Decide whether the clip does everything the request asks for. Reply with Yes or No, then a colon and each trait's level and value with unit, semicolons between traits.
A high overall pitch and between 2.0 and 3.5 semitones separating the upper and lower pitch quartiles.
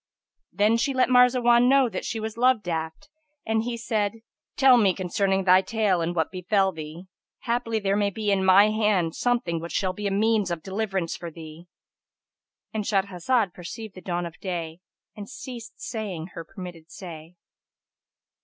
No: high, 200 Hz; average, 4.2 semitones